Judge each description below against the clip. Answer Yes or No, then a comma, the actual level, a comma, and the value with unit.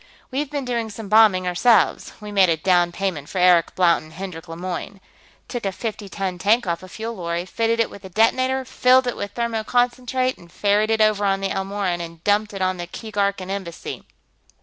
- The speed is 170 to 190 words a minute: No, average, 200 wpm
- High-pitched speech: Yes, high, 200 Hz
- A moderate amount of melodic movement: Yes, average, 3.8 semitones